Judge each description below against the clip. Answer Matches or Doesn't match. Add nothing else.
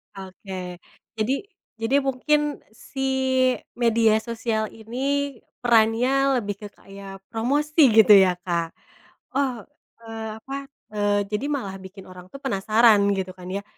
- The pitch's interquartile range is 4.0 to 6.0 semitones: Matches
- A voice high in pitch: Matches